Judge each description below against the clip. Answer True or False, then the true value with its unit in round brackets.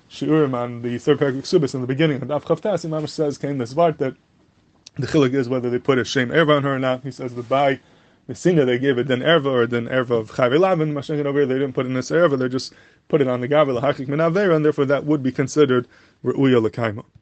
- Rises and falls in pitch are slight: False (3.0 semitones)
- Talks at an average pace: False (225 wpm)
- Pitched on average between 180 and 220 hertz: False (135 Hz)